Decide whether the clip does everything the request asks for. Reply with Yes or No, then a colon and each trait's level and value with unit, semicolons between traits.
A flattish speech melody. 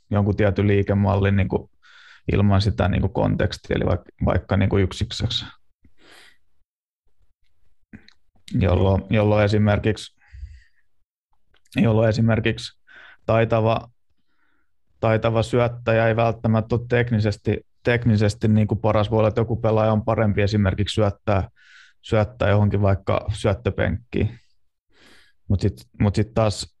Yes: narrow, 2.0 semitones